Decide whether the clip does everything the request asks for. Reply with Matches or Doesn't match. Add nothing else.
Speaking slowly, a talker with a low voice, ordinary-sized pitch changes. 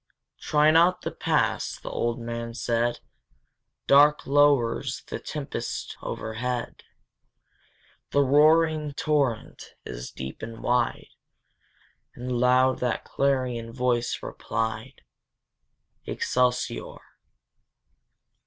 Matches